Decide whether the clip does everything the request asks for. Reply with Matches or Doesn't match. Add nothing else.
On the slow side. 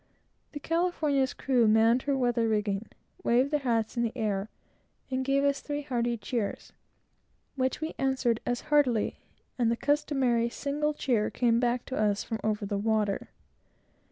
Doesn't match